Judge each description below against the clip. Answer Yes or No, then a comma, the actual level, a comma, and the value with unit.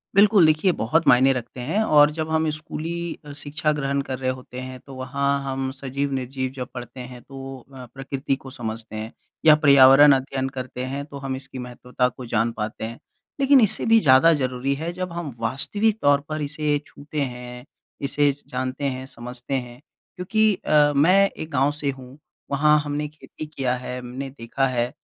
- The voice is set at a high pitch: No, low, 135 Hz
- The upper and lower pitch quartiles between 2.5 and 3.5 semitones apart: Yes, average, 2.9 semitones